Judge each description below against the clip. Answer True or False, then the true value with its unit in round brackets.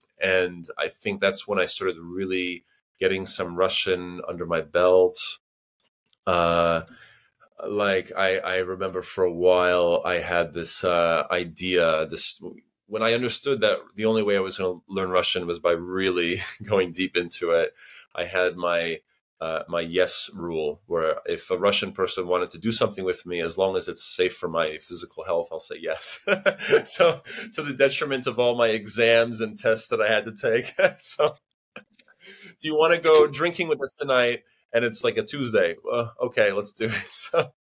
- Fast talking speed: False (180 wpm)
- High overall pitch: False (95 Hz)